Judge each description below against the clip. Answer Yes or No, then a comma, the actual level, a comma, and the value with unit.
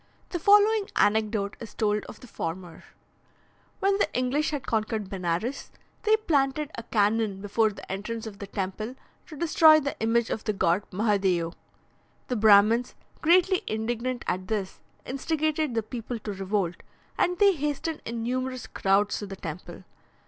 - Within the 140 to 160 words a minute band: Yes, average, 155 wpm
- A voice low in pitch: No, high, 225 Hz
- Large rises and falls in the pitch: Yes, wide, 5.9 semitones